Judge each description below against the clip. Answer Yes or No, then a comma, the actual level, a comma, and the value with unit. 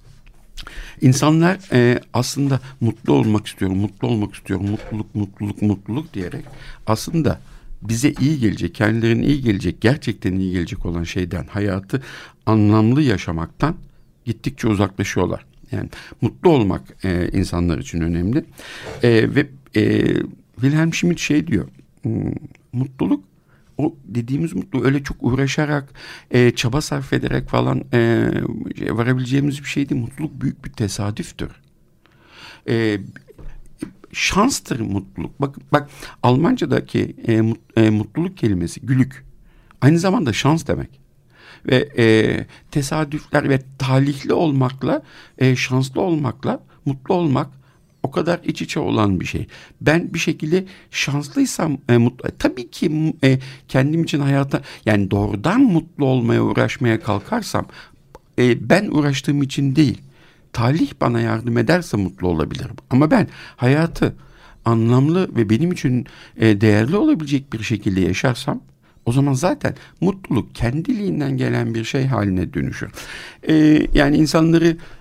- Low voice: Yes, low, 130 Hz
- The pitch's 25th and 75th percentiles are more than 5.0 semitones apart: Yes, wide, 5.5 semitones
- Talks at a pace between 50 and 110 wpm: No, average, 120 wpm